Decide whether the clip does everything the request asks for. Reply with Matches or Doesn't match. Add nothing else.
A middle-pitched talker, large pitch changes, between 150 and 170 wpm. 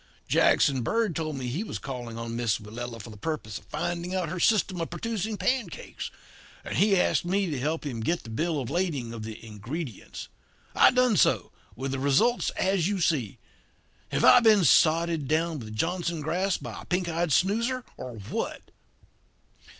Doesn't match